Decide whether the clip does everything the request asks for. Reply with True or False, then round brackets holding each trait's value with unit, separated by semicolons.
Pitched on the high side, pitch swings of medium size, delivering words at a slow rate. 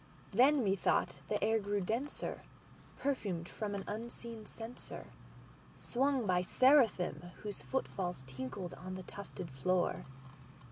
True (205 Hz; 4.8 semitones; 120 wpm)